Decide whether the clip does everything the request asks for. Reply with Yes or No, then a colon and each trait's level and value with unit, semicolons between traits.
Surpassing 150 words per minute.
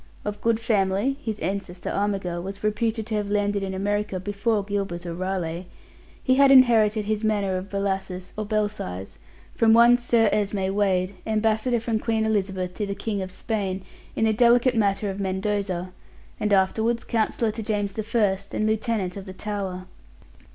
Yes: average, 165 wpm